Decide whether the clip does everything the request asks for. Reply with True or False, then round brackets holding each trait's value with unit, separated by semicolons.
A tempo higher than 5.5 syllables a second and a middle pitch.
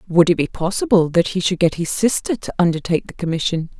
True (6.2 syllables/s; 175 Hz)